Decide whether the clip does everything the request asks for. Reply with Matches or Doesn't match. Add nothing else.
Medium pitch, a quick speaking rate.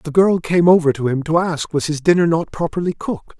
Matches